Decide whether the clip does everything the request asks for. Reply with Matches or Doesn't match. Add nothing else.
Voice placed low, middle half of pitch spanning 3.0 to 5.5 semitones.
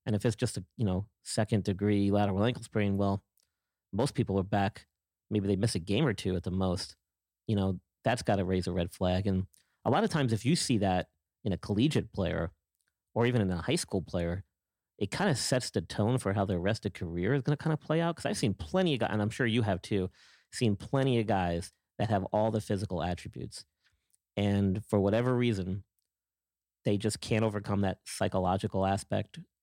Matches